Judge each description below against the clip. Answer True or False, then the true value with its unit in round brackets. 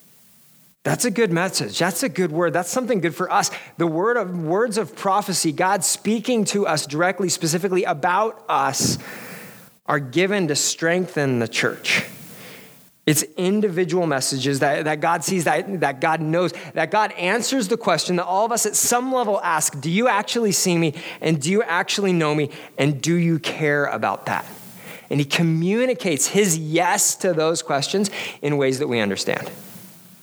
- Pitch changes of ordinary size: True (4.2 semitones)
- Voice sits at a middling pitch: True (175 Hz)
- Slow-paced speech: False (175 wpm)